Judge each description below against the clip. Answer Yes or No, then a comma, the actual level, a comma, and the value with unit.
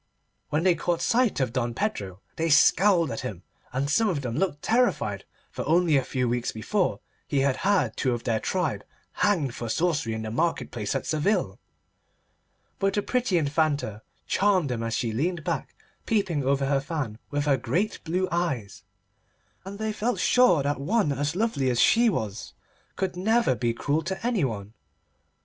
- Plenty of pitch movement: Yes, wide, 7.1 semitones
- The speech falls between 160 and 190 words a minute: Yes, average, 175 wpm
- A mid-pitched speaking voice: Yes, medium, 150 Hz